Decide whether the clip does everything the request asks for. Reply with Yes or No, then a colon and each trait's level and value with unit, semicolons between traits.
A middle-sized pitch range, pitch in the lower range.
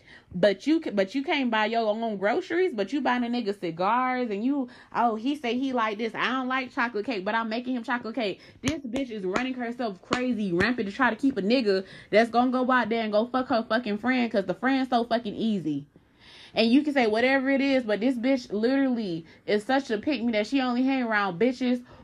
No: average, 3.6 semitones; high, 235 Hz